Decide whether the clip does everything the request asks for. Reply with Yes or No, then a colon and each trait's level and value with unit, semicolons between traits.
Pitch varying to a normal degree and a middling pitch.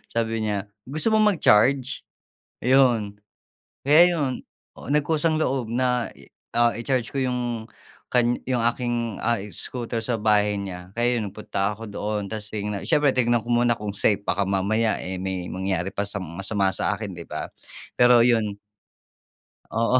No: average, 3.4 semitones; low, 115 Hz